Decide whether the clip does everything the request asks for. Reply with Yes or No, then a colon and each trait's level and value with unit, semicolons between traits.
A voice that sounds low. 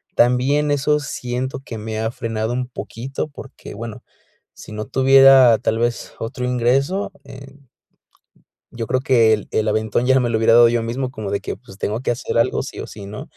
Yes: low, 120 Hz